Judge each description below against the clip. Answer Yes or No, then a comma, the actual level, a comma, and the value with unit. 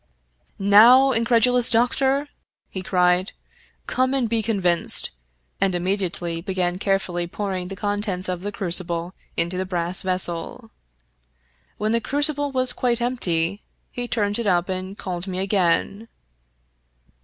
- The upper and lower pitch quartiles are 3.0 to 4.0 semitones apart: No, average, 4.4 semitones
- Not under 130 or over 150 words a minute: Yes, average, 140 wpm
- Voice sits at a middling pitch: No, high, 195 Hz